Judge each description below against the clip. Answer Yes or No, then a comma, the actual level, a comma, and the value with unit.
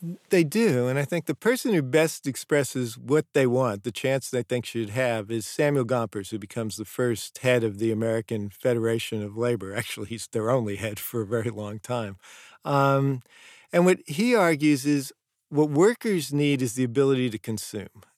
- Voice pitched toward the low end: Yes, low, 125 Hz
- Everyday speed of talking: Yes, average, 190 wpm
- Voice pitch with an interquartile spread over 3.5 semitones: Yes, average, 4.4 semitones